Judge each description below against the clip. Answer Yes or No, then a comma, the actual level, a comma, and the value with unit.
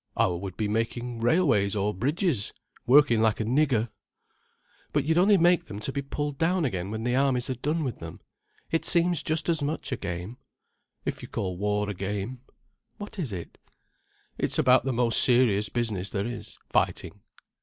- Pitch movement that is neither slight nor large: No, wide, 6.0 semitones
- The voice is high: No, low, 120 Hz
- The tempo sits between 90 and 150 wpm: No, average, 180 wpm